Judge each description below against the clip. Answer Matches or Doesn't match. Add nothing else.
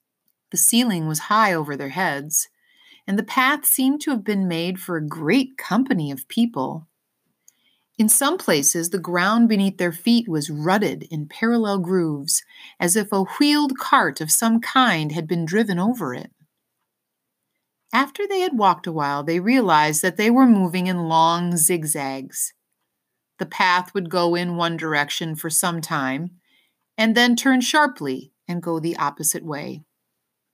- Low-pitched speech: Doesn't match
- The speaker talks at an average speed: Matches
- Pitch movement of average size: Doesn't match